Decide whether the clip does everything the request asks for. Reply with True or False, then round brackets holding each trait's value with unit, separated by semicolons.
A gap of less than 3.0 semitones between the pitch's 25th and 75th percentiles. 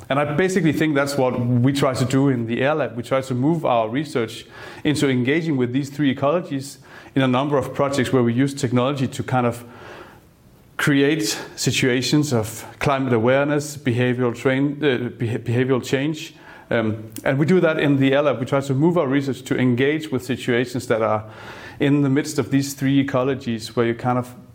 True (2.5 semitones)